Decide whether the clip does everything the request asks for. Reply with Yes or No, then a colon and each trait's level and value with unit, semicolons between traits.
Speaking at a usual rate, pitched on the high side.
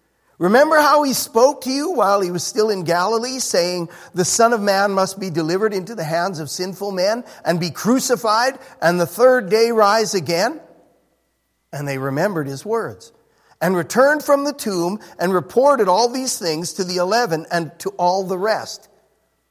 Yes: average, 180 wpm; high, 195 Hz